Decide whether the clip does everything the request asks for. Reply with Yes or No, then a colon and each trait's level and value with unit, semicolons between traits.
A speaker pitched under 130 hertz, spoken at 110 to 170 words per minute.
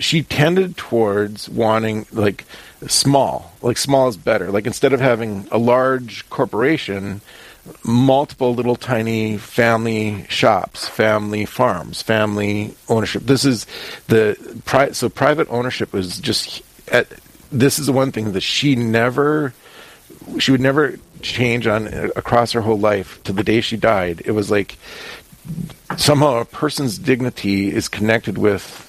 Yes: low, 115 Hz; average, 140 wpm